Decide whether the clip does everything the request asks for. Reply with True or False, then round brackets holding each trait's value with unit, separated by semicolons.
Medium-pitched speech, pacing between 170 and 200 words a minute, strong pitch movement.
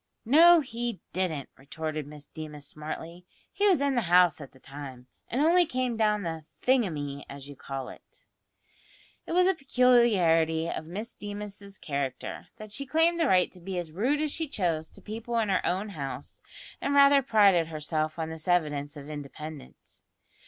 True (180 Hz; 175 wpm; 7.7 semitones)